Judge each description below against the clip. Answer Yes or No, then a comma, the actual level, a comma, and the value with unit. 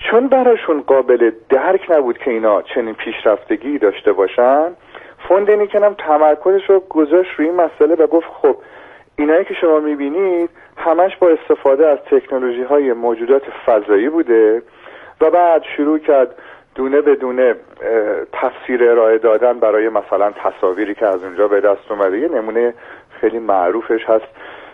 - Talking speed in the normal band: Yes, average, 145 wpm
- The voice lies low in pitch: No, medium, 170 Hz